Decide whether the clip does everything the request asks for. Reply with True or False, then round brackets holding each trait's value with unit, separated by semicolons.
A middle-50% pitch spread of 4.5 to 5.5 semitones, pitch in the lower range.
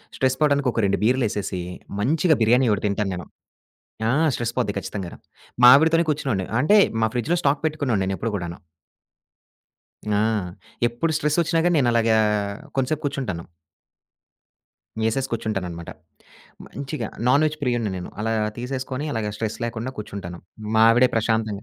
True (5.1 semitones; 120 Hz)